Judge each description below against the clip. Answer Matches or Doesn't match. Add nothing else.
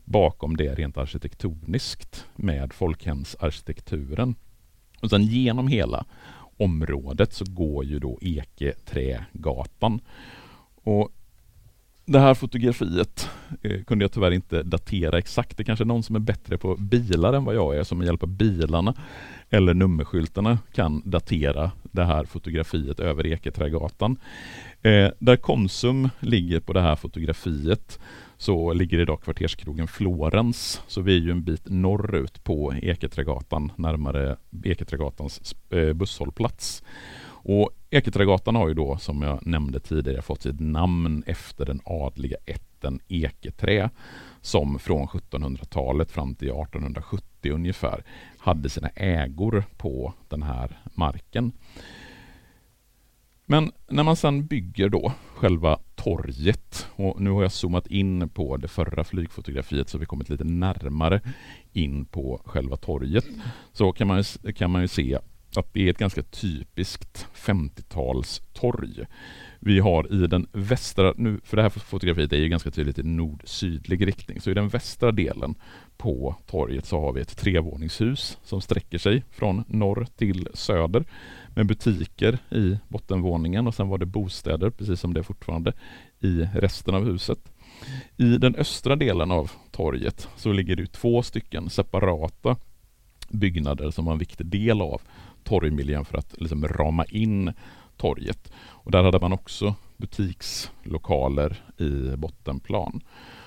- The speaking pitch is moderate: Doesn't match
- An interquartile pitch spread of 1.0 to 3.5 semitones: Doesn't match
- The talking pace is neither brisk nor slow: Matches